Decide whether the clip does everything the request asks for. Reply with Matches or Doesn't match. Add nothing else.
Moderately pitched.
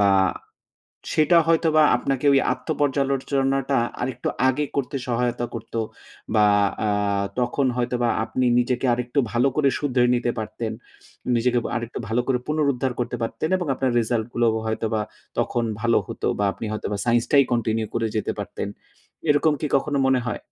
Doesn't match